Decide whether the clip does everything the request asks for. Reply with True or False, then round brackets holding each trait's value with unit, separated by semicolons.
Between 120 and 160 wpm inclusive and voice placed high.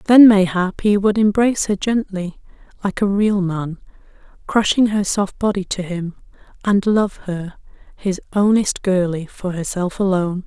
True (150 wpm; 195 Hz)